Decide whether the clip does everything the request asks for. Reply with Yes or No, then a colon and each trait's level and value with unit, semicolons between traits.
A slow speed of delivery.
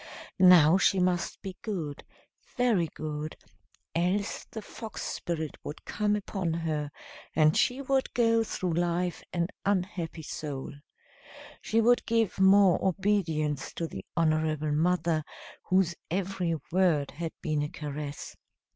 Yes: slow, 130 wpm